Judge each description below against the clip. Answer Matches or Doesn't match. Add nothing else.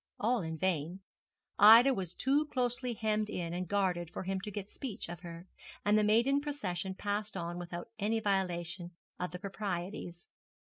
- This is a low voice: Doesn't match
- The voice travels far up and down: Doesn't match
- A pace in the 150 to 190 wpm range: Matches